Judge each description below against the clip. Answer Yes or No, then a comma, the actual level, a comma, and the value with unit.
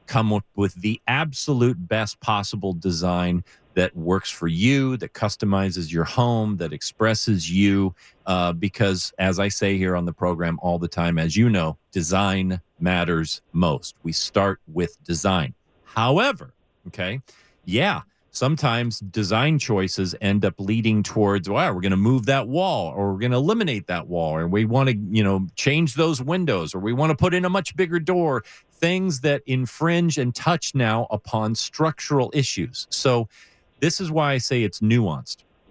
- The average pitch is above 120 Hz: No, low, 110 Hz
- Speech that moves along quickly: No, average, 170 wpm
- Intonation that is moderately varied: No, wide, 6.5 semitones